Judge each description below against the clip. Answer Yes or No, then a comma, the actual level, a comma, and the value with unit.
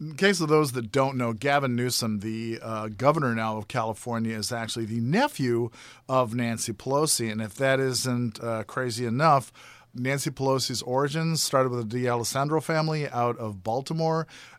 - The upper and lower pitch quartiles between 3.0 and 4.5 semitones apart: Yes, average, 3.5 semitones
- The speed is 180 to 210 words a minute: No, average, 165 wpm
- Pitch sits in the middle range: No, low, 125 Hz